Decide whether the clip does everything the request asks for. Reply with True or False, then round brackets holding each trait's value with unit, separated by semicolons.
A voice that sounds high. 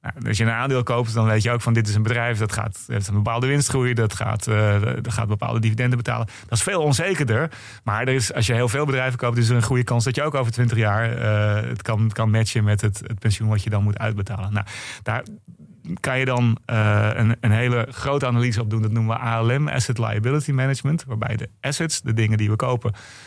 False (115 Hz)